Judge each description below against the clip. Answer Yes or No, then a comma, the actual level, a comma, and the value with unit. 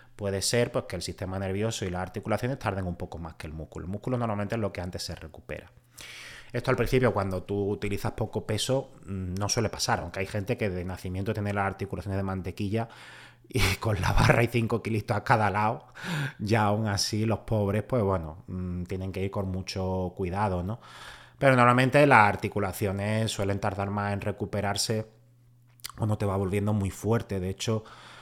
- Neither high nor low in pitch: No, low, 105 Hz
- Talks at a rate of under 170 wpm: No, fast, 190 wpm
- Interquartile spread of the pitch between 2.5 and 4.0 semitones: Yes, average, 3.0 semitones